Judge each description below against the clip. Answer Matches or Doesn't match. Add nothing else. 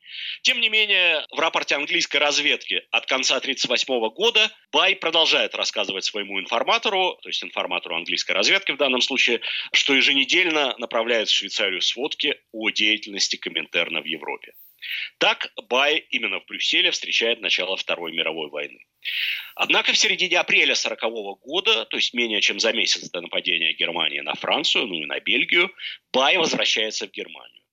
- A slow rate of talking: Doesn't match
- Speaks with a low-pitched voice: Doesn't match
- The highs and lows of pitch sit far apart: Matches